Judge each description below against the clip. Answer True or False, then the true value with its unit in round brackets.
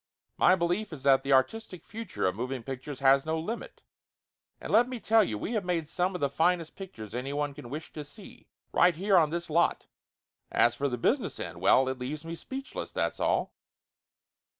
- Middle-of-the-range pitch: True (160 Hz)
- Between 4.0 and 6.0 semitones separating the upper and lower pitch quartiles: True (5.5 semitones)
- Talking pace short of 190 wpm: False (195 wpm)